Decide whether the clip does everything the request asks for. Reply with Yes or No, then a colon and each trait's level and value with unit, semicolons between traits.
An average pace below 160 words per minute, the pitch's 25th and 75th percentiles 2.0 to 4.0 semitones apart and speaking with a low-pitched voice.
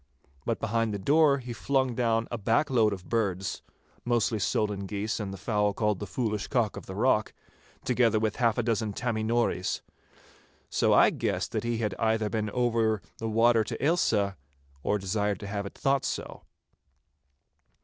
No: average, 170 wpm; narrow, 2.5 semitones; low, 110 Hz